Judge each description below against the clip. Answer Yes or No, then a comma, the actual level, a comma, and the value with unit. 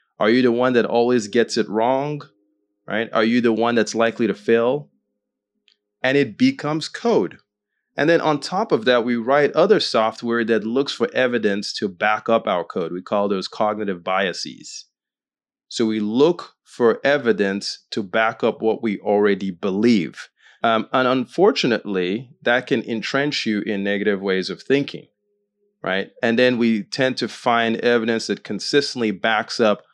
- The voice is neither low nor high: No, low, 115 Hz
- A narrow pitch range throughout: No, average, 3.9 semitones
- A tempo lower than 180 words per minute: Yes, average, 165 wpm